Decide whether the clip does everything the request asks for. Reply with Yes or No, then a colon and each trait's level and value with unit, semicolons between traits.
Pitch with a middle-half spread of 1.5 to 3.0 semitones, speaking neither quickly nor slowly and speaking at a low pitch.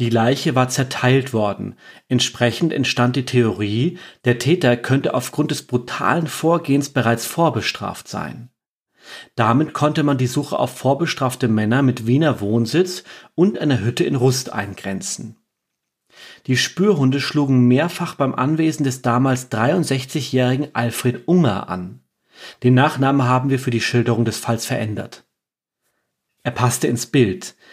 No: average, 3.5 semitones; average, 135 wpm; low, 130 Hz